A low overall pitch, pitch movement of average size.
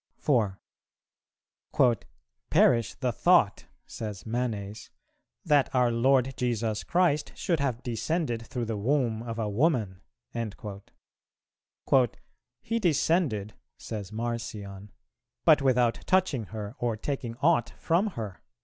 Yes: low, 120 Hz; average, 4.7 semitones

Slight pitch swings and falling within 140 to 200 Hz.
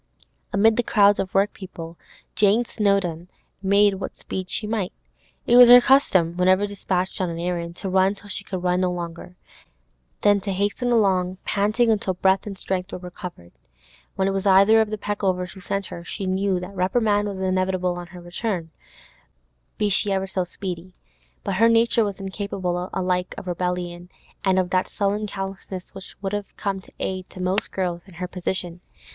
Yes: narrow, 2.0 semitones; high, 190 Hz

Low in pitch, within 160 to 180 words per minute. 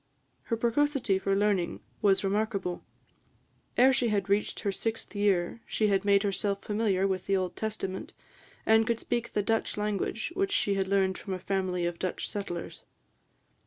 No: high, 200 Hz; average, 165 wpm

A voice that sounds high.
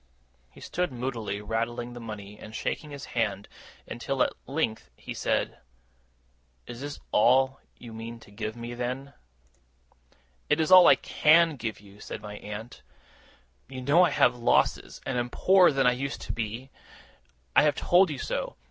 No: low, 120 Hz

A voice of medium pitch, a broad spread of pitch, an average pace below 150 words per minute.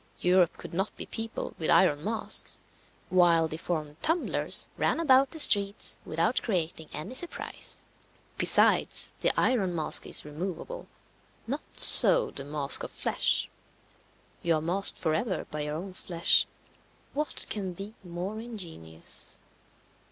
Yes: medium, 180 Hz; wide, 5.7 semitones; slow, 135 wpm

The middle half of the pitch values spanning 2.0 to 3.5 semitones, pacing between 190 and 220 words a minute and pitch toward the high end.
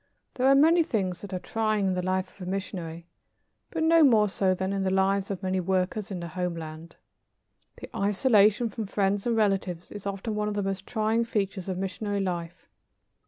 Yes: narrow, 2.5 semitones; average, 200 wpm; high, 195 Hz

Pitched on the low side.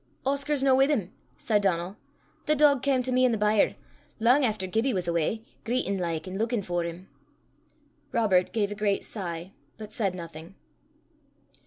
No: high, 210 Hz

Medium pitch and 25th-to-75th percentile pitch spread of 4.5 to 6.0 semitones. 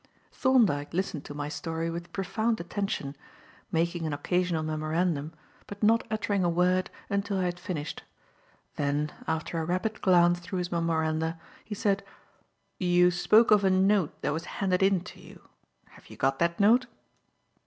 No: medium, 175 Hz; average, 3.3 semitones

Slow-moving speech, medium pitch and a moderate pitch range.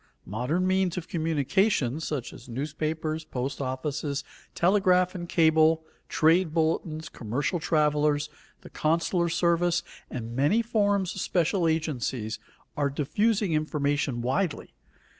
Yes: slow, 115 wpm; medium, 160 Hz; average, 3.6 semitones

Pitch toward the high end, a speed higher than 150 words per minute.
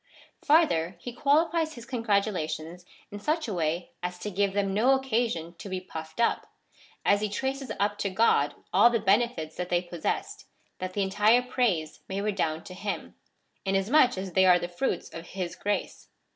Yes: high, 200 Hz; average, 175 wpm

